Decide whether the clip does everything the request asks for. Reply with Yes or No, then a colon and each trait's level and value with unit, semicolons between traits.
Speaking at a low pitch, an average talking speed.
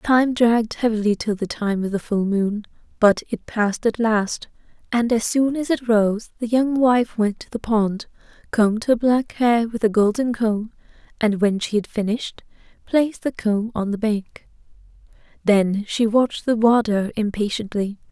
No: high, 220 Hz; average, 175 wpm